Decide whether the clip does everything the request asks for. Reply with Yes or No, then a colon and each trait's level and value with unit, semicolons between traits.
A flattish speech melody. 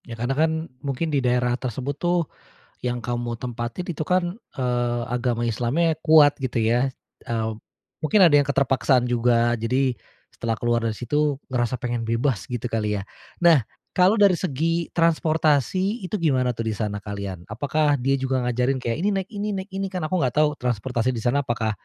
No: average, 4.7 semitones